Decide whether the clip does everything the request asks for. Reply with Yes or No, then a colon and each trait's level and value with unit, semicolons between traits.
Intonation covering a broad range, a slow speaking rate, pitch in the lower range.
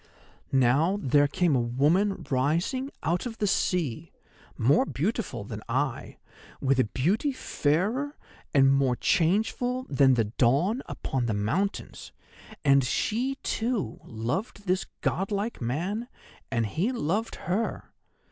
No: wide, 8.1 semitones; slow, 125 wpm; medium, 160 Hz